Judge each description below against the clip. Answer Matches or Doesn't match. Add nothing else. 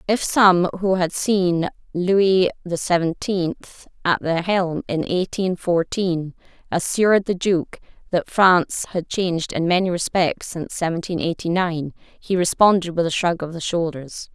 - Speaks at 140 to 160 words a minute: Matches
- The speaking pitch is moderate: Matches